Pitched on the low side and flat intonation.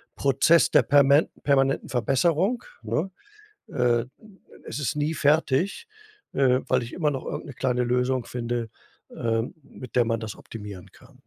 No: low, 130 Hz; average, 3.4 semitones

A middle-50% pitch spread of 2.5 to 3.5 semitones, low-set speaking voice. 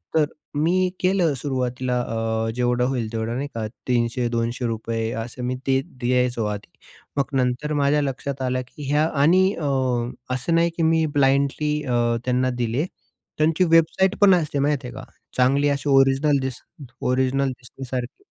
Yes: average, 3.1 semitones; low, 130 Hz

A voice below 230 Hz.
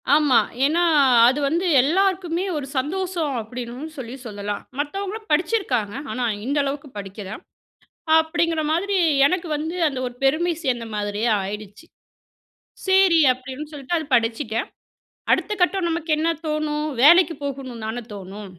No: very high, 290 Hz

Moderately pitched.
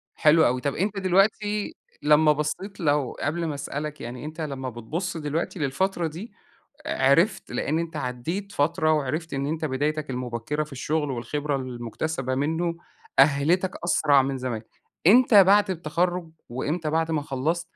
Yes: medium, 155 Hz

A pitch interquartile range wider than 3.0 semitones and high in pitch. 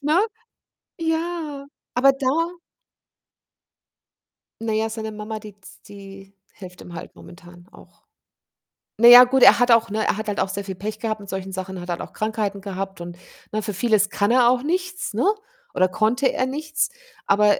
Yes: average, 4.5 semitones; high, 215 Hz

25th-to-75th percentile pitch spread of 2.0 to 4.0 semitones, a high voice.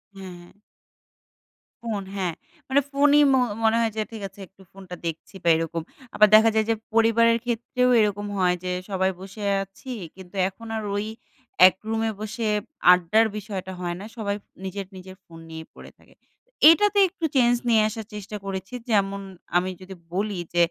Yes: average, 3.2 semitones; high, 205 Hz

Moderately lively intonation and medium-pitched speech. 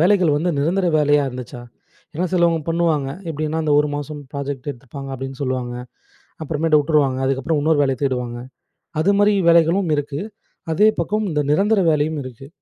Yes: average, 3.5 semitones; medium, 150 Hz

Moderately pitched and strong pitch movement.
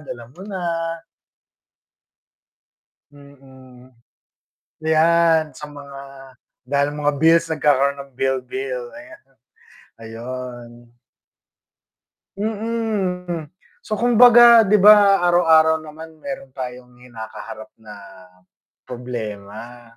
Yes: medium, 145 Hz; wide, 5.8 semitones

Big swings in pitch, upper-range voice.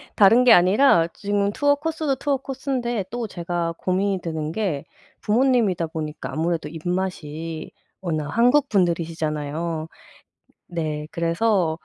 No: wide, 6.2 semitones; medium, 180 Hz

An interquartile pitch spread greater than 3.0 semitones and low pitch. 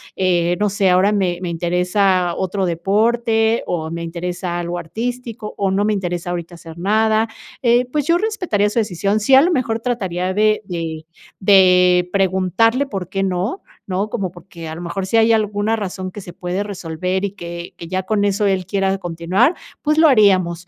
No: average, 3.4 semitones; high, 190 Hz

